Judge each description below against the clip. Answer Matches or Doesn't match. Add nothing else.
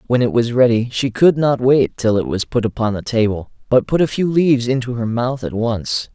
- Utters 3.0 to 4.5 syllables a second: Doesn't match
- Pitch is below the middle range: Matches